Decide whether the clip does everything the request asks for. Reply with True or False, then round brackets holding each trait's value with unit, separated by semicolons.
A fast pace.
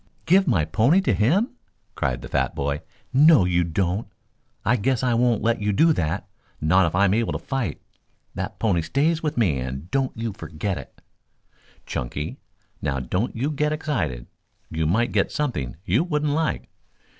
False (175 wpm)